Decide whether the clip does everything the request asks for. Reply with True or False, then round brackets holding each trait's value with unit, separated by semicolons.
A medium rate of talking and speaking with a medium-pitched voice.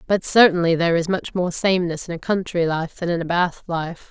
False (235 wpm; 175 Hz)